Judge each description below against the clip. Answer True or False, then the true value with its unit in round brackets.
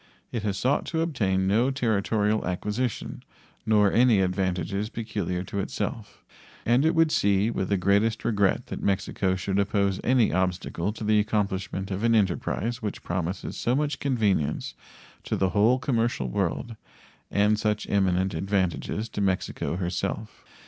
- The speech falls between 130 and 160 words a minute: True (150 wpm)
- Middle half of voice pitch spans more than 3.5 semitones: False (3.2 semitones)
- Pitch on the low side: True (100 Hz)